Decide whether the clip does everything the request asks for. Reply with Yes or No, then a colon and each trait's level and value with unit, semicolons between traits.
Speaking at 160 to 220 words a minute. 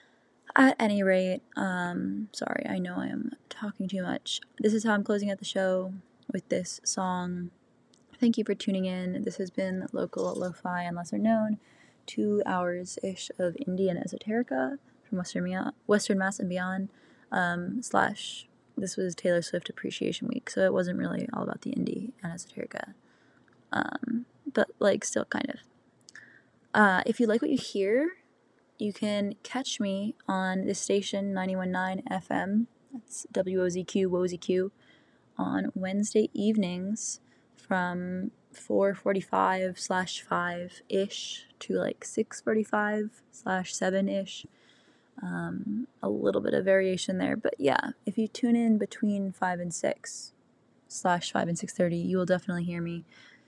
No: average, 145 wpm